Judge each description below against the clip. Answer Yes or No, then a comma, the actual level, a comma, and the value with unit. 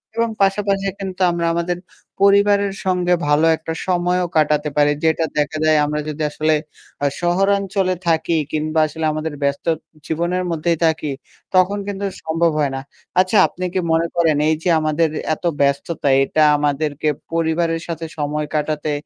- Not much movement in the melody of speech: No, average, 3.0 semitones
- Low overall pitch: No, medium, 165 Hz